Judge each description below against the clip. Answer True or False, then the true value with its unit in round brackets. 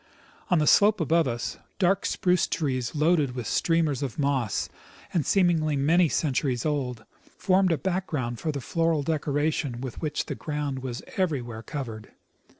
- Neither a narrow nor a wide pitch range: True (4.4 semitones)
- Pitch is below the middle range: False (150 Hz)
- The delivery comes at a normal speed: True (150 wpm)